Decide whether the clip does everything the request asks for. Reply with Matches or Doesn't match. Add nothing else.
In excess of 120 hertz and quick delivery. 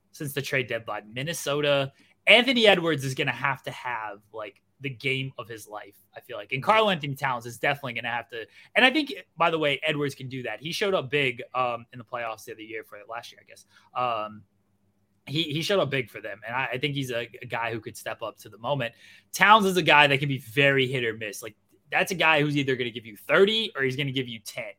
Matches